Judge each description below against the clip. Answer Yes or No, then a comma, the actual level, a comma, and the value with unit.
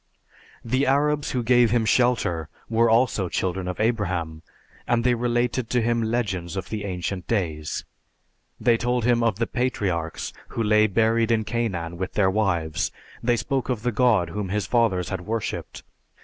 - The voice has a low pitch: Yes, low, 110 Hz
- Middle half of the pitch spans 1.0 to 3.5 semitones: No, average, 4.4 semitones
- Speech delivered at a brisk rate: No, average, 165 wpm